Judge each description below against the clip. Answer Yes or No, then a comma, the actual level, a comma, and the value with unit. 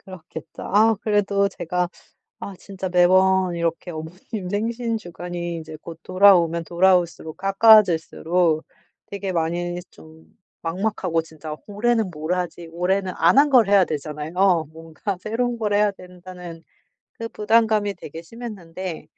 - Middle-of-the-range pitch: Yes, medium, 180 Hz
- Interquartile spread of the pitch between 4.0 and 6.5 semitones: No, average, 3.4 semitones